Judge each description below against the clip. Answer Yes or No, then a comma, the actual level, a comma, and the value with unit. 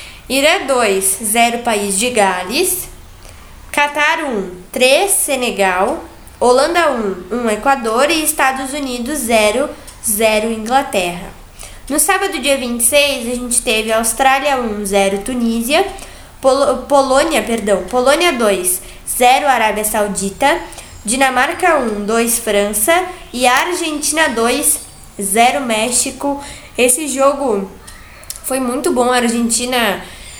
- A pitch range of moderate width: Yes, average, 4.2 semitones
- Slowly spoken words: Yes, slow, 115 wpm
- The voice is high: Yes, very high, 250 Hz